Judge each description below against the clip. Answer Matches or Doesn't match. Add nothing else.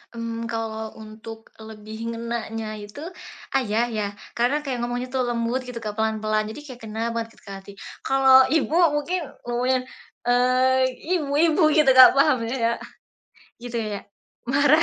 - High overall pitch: Matches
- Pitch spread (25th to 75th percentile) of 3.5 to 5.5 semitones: Doesn't match